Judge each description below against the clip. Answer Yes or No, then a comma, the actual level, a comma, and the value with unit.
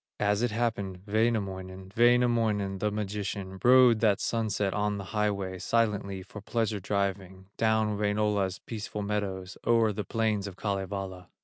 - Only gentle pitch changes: Yes, narrow, 2.2 semitones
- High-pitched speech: No, low, 105 Hz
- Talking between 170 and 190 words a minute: No, slow, 135 wpm